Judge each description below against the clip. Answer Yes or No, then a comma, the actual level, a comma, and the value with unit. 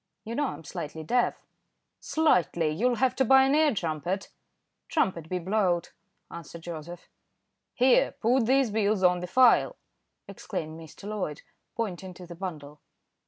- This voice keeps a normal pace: Yes, average, 145 wpm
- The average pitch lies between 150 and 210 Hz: Yes, medium, 185 Hz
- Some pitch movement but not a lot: No, wide, 6.3 semitones